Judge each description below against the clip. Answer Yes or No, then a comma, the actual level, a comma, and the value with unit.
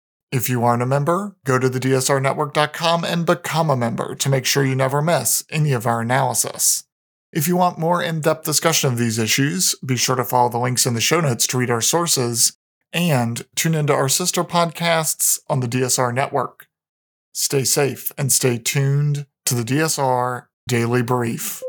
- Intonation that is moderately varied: Yes, average, 4.4 semitones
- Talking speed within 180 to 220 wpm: Yes, average, 185 wpm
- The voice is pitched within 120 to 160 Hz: Yes, medium, 140 Hz